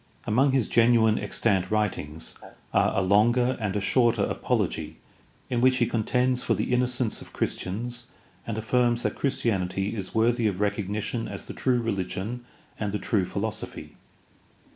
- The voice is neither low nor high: No, low, 110 Hz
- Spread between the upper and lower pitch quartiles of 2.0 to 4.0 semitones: Yes, average, 3.1 semitones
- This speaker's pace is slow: No, average, 150 wpm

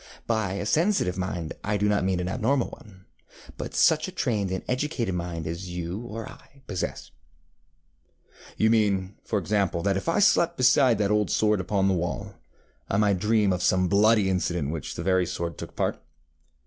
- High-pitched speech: No, low, 100 Hz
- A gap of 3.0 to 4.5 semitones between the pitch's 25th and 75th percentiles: Yes, average, 3.5 semitones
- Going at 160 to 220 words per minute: Yes, average, 185 wpm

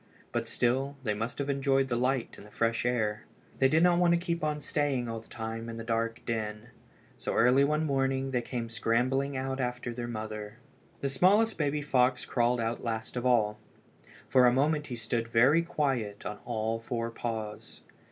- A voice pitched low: Yes, low, 125 Hz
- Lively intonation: No, average, 3.2 semitones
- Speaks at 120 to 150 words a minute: No, average, 190 wpm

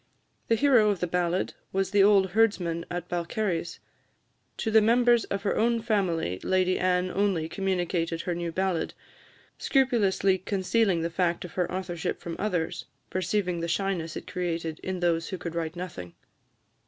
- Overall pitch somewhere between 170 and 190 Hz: Yes, medium, 185 Hz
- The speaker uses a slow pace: No, average, 160 wpm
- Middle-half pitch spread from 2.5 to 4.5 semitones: Yes, average, 2.9 semitones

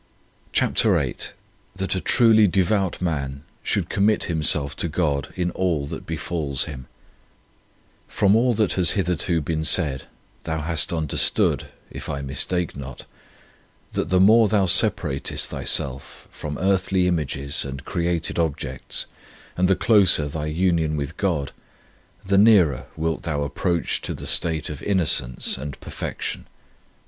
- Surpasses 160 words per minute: No, average, 140 wpm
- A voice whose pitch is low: Yes, very low, 80 Hz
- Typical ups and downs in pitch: Yes, average, 4.4 semitones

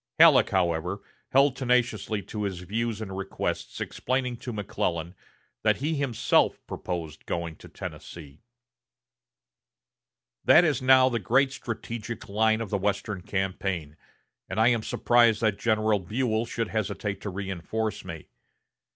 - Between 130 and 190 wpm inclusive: Yes, slow, 135 wpm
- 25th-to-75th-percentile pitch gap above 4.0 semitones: No, average, 3.7 semitones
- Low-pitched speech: Yes, low, 110 Hz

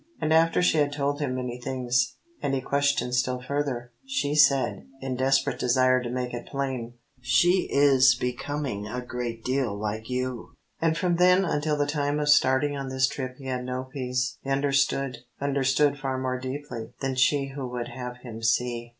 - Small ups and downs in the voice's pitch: Yes, narrow, 2.3 semitones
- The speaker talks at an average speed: Yes, average, 185 wpm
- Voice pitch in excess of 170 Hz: No, low, 130 Hz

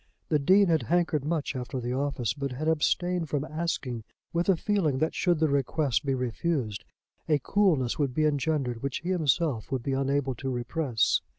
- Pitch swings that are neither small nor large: Yes, average, 3.9 semitones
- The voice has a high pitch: No, medium, 145 Hz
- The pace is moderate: Yes, average, 185 wpm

